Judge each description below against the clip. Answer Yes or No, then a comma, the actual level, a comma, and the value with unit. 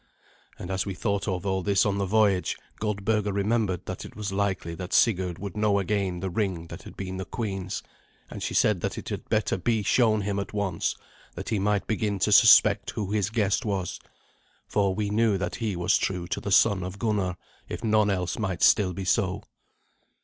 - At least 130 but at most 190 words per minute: No, fast, 205 wpm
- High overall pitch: No, low, 100 Hz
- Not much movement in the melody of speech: Yes, narrow, 2.2 semitones